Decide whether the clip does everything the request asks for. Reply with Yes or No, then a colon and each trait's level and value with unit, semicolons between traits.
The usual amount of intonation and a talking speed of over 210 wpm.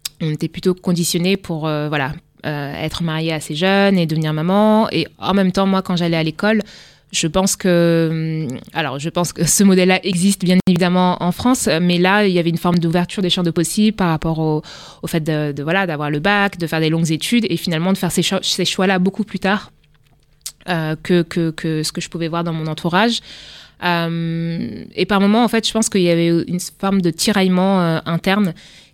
Yes: average, 3.0 semitones; fast, 220 wpm